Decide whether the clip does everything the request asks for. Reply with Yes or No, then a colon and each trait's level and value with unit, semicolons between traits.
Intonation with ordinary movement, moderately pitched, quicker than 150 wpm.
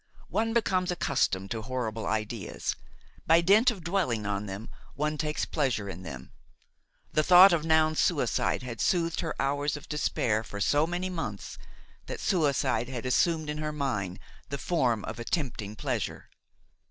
No: wide, 7.1 semitones; medium, 145 Hz; average, 160 wpm